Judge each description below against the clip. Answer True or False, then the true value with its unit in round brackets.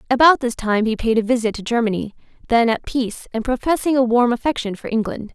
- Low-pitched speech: False (235 Hz)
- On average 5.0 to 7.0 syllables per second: True (6.1 syllables/s)